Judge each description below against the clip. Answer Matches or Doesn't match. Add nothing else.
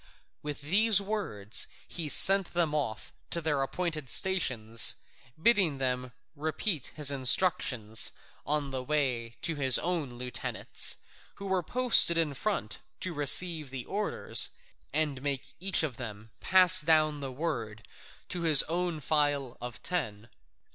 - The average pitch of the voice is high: Doesn't match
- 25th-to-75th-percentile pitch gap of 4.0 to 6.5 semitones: Matches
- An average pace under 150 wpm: Matches